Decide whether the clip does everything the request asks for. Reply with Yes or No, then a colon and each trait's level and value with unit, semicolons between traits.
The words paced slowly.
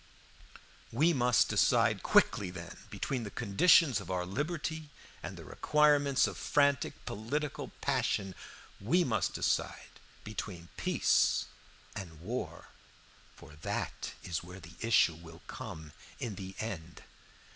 Yes: slow, 125 wpm